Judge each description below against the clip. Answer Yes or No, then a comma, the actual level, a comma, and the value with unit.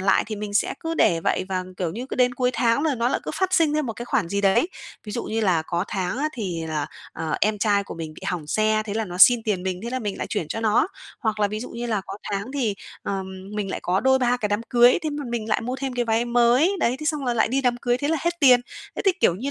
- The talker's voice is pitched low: No, high, 225 Hz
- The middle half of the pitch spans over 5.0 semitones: No, average, 4.1 semitones